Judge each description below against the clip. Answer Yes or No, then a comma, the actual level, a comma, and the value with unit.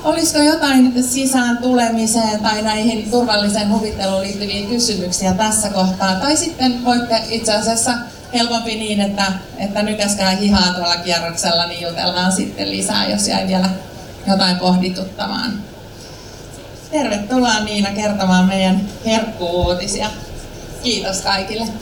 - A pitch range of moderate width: Yes, average, 3.4 semitones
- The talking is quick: No, average, 115 wpm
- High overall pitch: Yes, high, 205 Hz